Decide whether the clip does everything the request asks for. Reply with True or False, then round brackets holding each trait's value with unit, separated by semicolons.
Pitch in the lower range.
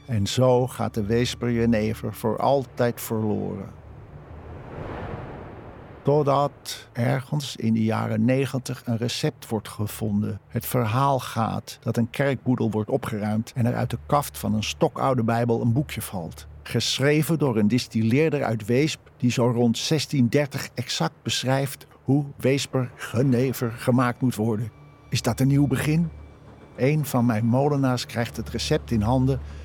True (125 Hz)